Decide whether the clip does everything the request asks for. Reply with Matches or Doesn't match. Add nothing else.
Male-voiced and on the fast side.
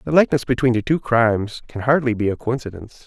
Matches